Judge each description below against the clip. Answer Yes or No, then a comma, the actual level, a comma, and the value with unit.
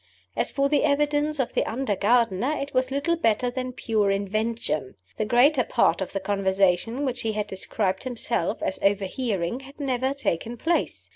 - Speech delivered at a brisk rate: No, average, 170 wpm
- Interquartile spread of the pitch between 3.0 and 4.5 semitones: No, average, 5.2 semitones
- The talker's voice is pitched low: No, high, 235 Hz